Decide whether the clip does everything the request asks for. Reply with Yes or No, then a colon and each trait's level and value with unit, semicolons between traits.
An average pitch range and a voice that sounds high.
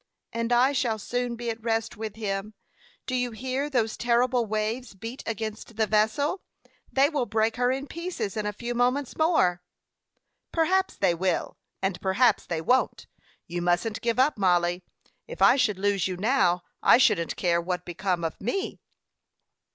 Yes: average, 4.6 semitones; high, 225 Hz